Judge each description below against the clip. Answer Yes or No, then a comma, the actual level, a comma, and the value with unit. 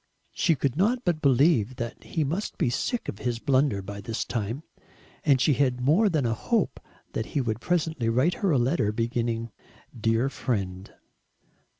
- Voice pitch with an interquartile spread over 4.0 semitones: Yes, wide, 5.5 semitones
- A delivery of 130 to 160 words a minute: No, average, 175 wpm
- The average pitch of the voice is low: Yes, low, 125 Hz